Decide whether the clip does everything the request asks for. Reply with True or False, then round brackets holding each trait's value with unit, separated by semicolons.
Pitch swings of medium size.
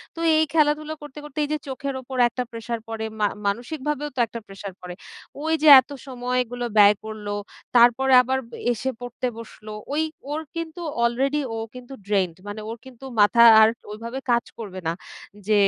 True (4.2 semitones)